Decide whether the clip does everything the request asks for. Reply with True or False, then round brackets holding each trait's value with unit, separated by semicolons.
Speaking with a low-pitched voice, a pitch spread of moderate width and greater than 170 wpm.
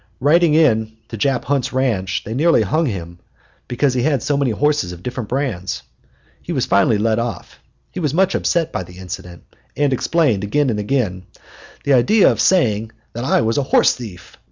False (120 Hz; 5.7 semitones; 185 wpm)